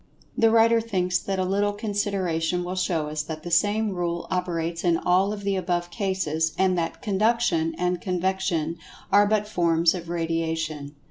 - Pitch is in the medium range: Yes, medium, 180 Hz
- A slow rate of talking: No, average, 170 wpm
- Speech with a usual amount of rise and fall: Yes, average, 3.2 semitones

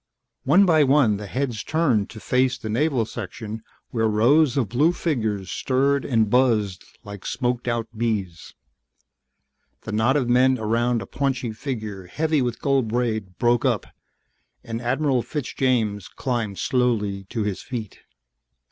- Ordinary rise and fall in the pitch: Yes, average, 3.6 semitones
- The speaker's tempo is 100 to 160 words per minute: Yes, average, 145 wpm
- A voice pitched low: Yes, low, 120 Hz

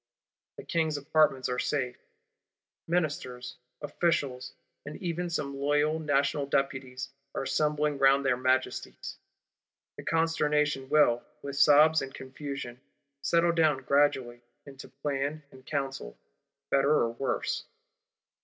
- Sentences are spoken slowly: Yes, slow, 115 wpm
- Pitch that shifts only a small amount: Yes, narrow, 2.3 semitones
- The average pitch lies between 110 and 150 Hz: Yes, medium, 140 Hz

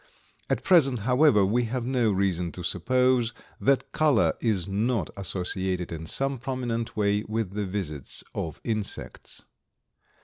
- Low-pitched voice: Yes, low, 110 Hz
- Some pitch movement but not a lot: Yes, average, 5.0 semitones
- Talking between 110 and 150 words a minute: Yes, slow, 135 wpm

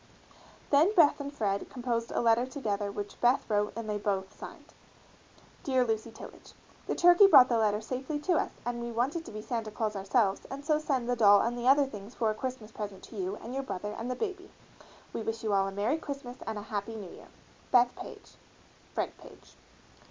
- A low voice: No, high, 235 Hz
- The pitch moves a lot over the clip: No, average, 4.2 semitones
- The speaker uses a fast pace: Yes, fast, 210 wpm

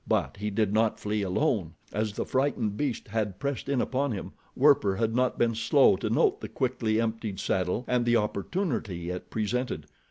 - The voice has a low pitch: Yes, low, 110 Hz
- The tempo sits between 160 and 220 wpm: Yes, average, 185 wpm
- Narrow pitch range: No, average, 3.7 semitones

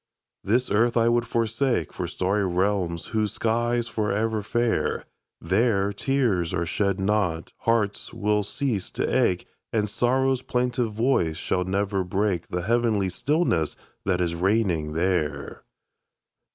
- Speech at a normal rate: No, slow, 130 wpm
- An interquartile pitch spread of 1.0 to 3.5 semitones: No, average, 4.3 semitones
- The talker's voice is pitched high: No, low, 105 Hz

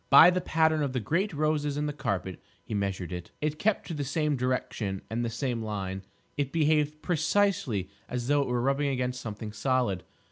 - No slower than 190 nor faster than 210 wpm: Yes, average, 200 wpm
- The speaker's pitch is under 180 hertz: Yes, low, 135 Hz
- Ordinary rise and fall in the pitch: No, wide, 5.7 semitones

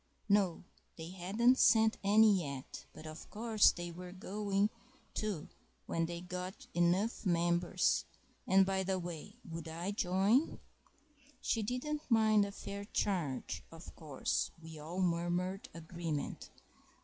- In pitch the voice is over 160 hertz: Yes, medium, 185 Hz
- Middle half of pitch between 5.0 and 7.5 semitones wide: No, average, 3.5 semitones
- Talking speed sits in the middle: No, slow, 130 wpm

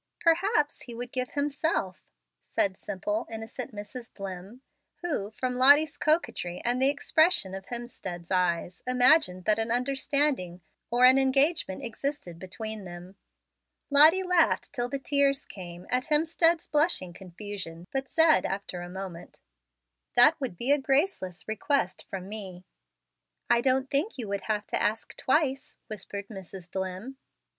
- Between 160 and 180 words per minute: No, average, 140 wpm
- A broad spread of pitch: Yes, wide, 6.8 semitones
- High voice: Yes, high, 240 Hz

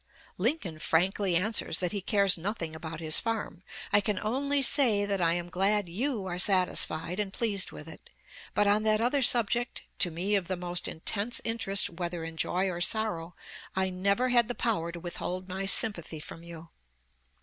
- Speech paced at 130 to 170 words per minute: No, average, 180 wpm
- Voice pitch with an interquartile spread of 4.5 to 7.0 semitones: No, average, 3.8 semitones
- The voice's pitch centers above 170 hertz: Yes, high, 190 Hz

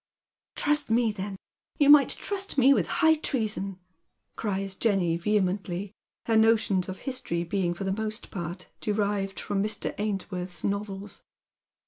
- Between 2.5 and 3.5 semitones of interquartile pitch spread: Yes, average, 2.8 semitones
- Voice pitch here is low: No, high, 205 Hz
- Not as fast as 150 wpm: Yes, average, 140 wpm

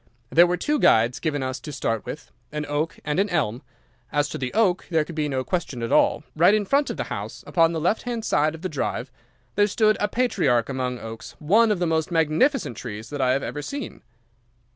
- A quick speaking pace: Yes, fast, 230 wpm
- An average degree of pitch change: No, wide, 6.6 semitones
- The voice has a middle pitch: Yes, medium, 155 Hz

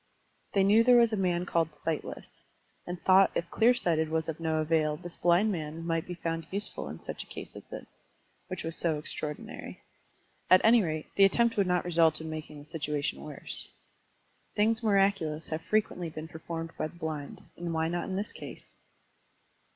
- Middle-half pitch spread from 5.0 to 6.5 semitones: No, average, 3.4 semitones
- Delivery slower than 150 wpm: No, average, 190 wpm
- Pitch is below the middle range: No, medium, 170 Hz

